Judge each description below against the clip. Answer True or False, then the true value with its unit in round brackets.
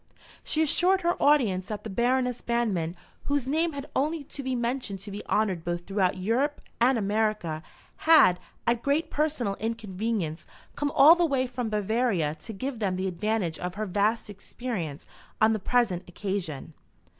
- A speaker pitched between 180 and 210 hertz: False (220 Hz)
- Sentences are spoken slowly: False (165 wpm)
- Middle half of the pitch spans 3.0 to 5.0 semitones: False (5.6 semitones)